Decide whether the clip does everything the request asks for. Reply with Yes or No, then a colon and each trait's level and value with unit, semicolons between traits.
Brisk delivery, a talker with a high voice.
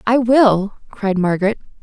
No: slow, 130 wpm; high, 215 Hz